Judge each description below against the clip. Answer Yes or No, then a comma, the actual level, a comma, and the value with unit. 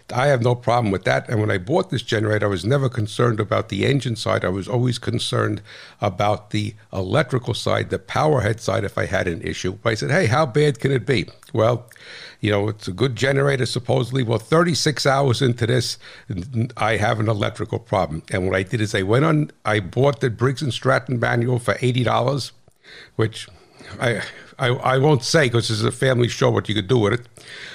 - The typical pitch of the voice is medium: No, low, 120 Hz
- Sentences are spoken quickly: Yes, fast, 215 wpm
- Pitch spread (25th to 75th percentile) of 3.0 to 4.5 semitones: Yes, average, 3.5 semitones